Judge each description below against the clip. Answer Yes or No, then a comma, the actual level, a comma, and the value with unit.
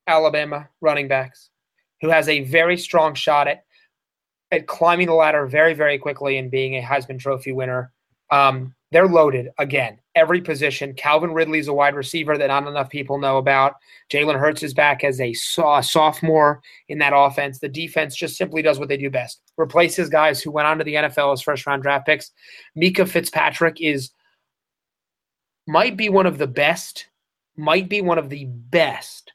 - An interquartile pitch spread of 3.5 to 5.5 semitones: No, narrow, 2.6 semitones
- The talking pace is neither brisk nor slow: Yes, average, 180 wpm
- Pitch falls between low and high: Yes, medium, 150 Hz